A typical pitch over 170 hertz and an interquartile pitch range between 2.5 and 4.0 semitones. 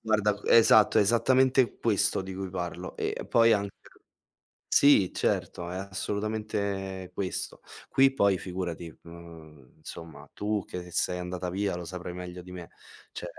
No: very low, 95 Hz; average, 2.9 semitones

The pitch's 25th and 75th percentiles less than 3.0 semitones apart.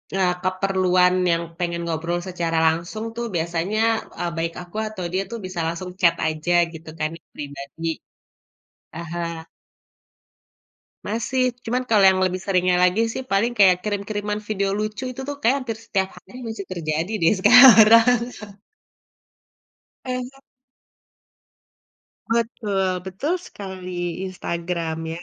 No: average, 4.1 semitones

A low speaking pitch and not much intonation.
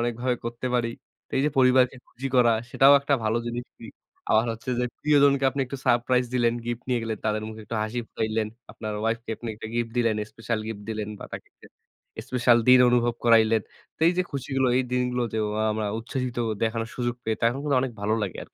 Yes: low, 120 Hz; narrow, 2.1 semitones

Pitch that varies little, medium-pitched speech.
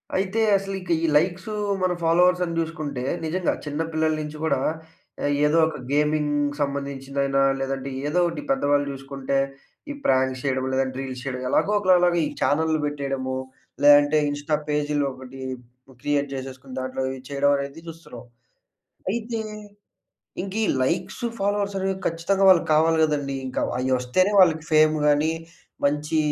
No: average, 3.5 semitones; medium, 150 Hz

